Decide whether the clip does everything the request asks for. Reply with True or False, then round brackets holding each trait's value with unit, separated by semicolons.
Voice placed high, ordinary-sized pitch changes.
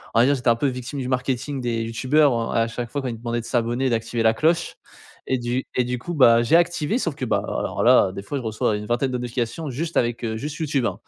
False (125 Hz; 3.3 semitones)